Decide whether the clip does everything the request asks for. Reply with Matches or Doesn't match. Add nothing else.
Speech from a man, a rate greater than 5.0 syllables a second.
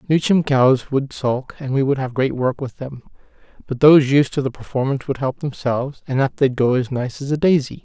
Matches